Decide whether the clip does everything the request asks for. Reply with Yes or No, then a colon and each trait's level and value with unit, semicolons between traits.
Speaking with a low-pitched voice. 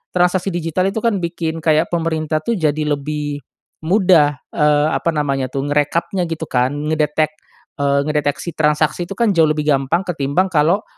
No: medium, 155 Hz